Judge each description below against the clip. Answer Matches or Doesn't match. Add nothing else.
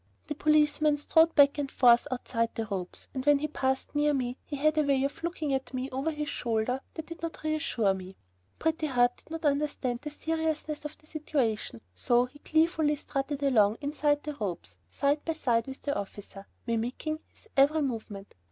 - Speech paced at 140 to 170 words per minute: Doesn't match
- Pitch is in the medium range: Doesn't match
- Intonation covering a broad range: Doesn't match